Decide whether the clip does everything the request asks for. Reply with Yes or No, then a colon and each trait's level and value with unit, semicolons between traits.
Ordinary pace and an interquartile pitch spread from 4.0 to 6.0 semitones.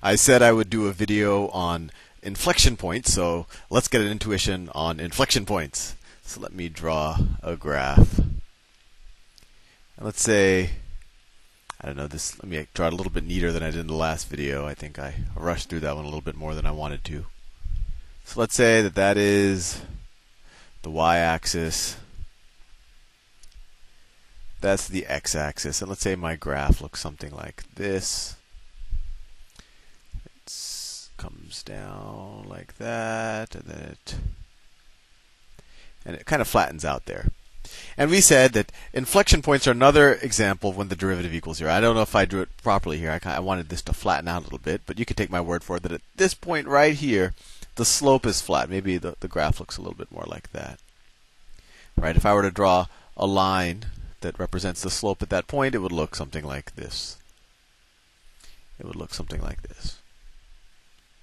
Yes: average, 180 wpm; average, 4.4 semitones